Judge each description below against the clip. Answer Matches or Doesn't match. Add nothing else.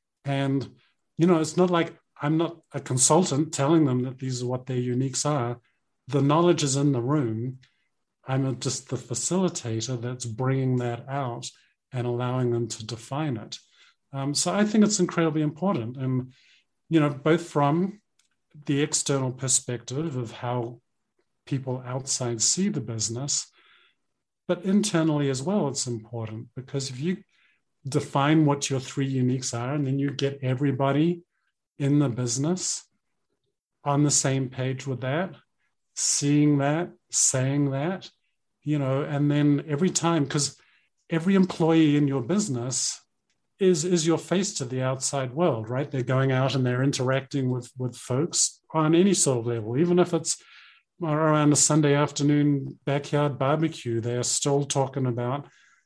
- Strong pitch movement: Doesn't match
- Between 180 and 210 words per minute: Doesn't match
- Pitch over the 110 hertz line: Matches